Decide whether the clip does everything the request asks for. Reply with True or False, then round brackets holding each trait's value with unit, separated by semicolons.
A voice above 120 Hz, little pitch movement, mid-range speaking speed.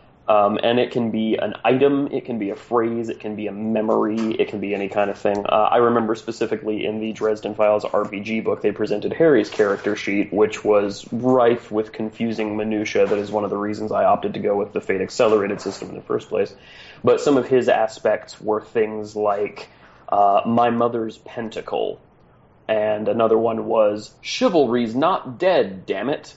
False (110 Hz; 1.6 semitones; 195 wpm)